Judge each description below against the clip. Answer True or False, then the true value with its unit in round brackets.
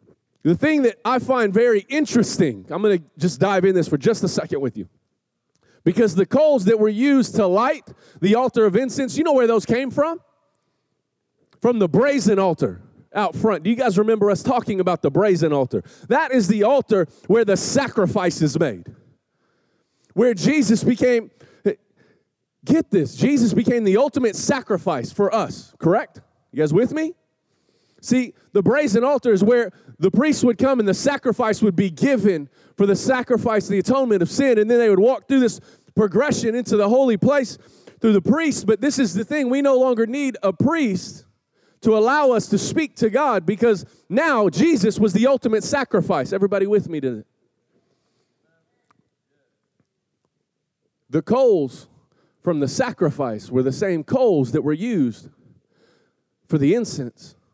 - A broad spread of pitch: False (5.0 semitones)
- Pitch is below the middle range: False (220 Hz)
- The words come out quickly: False (170 wpm)